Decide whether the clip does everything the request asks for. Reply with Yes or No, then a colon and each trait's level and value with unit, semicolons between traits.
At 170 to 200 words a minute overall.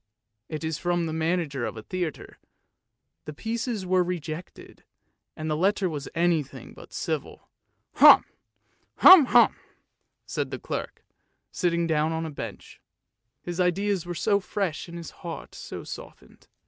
No: average, 150 wpm